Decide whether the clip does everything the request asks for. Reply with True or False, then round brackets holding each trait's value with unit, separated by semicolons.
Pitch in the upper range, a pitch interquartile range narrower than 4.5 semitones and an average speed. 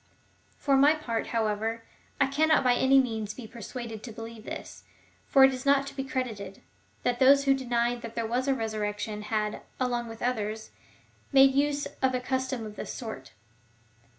True (245 Hz; 3.3 semitones; 180 wpm)